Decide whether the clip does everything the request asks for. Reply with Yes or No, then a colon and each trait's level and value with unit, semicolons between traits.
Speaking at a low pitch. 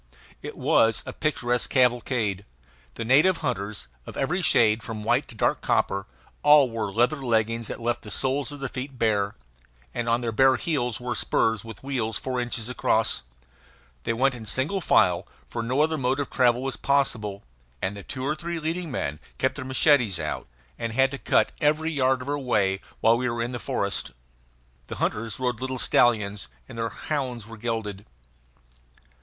Yes: low, 120 Hz